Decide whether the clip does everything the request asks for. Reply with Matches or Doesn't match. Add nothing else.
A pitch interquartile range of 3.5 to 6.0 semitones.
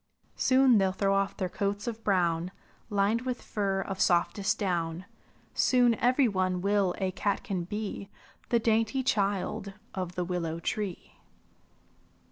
Doesn't match